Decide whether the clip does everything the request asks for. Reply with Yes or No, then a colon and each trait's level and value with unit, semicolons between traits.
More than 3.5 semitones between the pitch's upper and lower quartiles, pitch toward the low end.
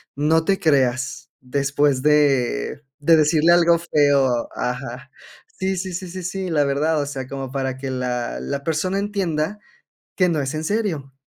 No: average, 4.2 semitones; medium, 145 Hz